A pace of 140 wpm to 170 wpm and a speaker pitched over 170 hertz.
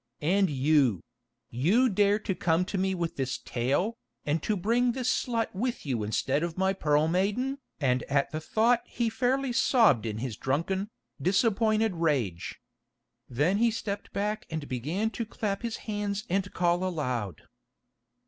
Yes: average, 155 wpm; medium, 185 Hz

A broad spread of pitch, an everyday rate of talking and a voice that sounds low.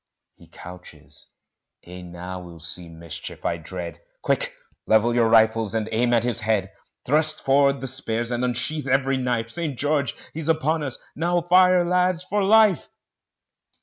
Yes: wide, 7.9 semitones; average, 155 wpm; low, 125 Hz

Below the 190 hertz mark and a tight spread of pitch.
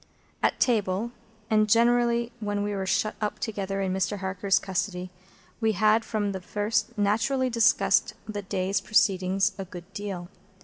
No: high, 205 Hz; narrow, 2.2 semitones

